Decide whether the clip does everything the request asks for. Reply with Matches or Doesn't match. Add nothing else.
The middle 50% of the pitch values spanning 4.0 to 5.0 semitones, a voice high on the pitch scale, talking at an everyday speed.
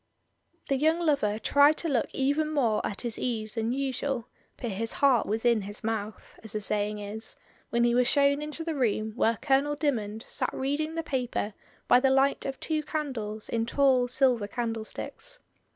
Matches